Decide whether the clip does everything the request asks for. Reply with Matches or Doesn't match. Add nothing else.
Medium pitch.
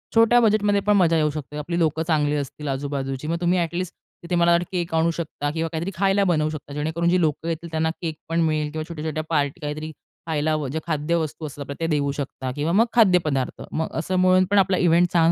Matches